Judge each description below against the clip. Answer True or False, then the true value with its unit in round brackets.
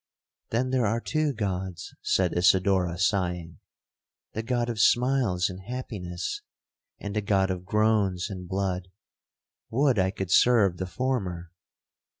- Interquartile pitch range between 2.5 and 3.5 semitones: False (4.4 semitones)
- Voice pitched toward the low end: True (100 Hz)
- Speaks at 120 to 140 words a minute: True (135 wpm)